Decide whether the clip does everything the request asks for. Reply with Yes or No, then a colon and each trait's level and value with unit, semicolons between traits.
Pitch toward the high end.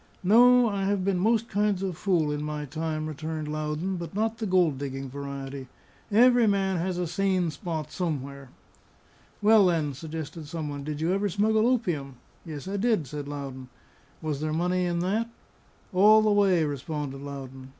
No: medium, 165 Hz